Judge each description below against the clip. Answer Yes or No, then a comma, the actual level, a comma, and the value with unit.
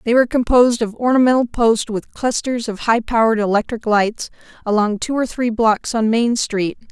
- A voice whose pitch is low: No, high, 230 Hz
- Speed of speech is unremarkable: Yes, average, 180 wpm